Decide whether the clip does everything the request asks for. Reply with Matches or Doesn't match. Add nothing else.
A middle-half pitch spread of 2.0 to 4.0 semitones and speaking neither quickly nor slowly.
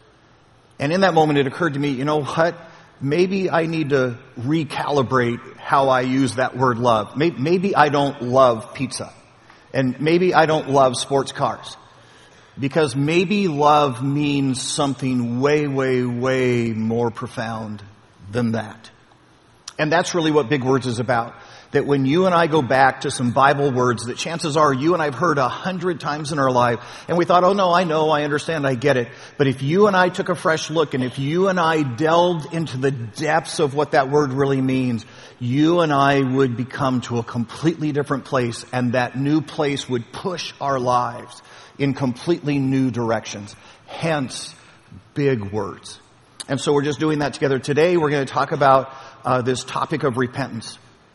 Matches